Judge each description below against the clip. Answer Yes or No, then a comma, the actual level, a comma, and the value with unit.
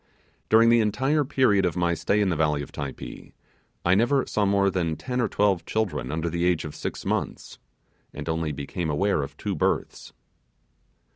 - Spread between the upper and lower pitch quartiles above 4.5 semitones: Yes, average, 5.0 semitones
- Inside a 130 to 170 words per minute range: No, average, 185 wpm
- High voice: No, very low, 90 Hz